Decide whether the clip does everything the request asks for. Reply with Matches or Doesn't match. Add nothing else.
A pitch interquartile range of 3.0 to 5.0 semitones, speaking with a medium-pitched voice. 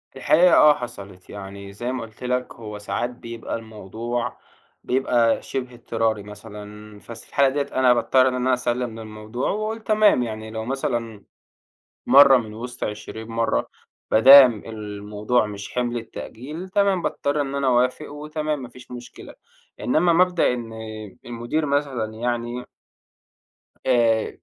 Doesn't match